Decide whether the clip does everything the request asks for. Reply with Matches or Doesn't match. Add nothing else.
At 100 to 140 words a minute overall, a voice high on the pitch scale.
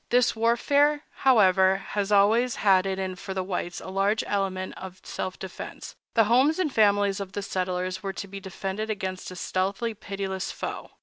Doesn't match